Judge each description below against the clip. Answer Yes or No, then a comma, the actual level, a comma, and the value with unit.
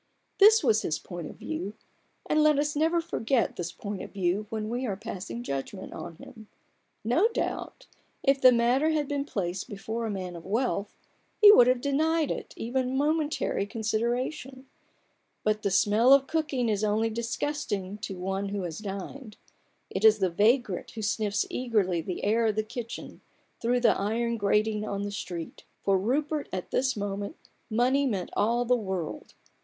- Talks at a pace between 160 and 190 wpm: Yes, average, 170 wpm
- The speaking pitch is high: Yes, high, 220 Hz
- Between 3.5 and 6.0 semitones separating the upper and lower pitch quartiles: Yes, average, 4.6 semitones